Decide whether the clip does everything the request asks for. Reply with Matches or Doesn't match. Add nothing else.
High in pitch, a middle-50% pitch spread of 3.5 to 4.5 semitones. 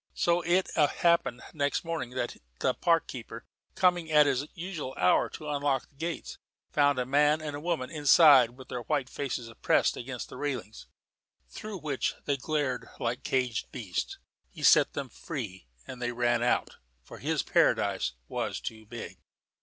Doesn't match